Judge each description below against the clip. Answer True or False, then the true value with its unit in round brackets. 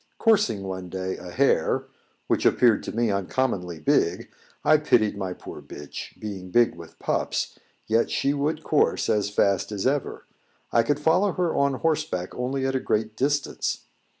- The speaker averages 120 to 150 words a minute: False (165 wpm)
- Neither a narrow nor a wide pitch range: False (6.6 semitones)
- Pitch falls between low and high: False (120 Hz)